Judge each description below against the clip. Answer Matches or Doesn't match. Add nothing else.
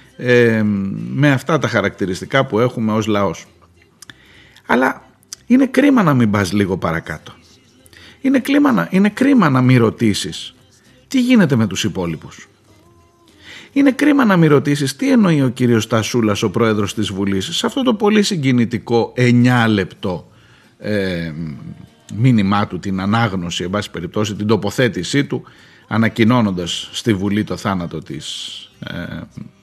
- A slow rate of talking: Doesn't match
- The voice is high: Doesn't match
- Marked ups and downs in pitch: Matches